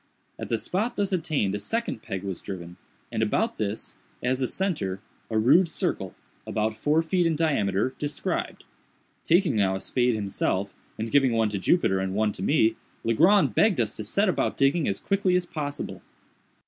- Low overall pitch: Yes, low, 125 Hz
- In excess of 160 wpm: Yes, average, 180 wpm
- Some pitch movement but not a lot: No, wide, 8.8 semitones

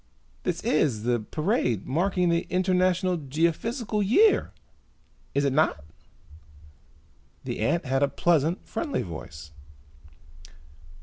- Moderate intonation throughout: No, wide, 5.7 semitones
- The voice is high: No, medium, 165 Hz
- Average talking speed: No, slow, 105 wpm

